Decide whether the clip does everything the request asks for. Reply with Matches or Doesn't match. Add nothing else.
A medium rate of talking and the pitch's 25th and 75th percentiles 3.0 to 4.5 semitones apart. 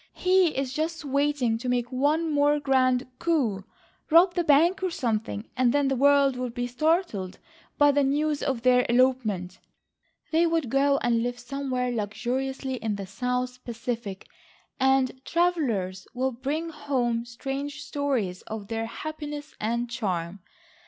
Matches